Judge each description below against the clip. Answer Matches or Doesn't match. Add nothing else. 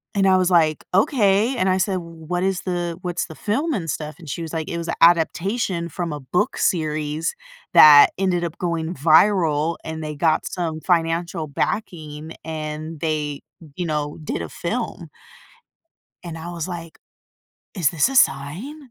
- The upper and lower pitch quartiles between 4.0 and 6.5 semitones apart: Doesn't match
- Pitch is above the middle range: Doesn't match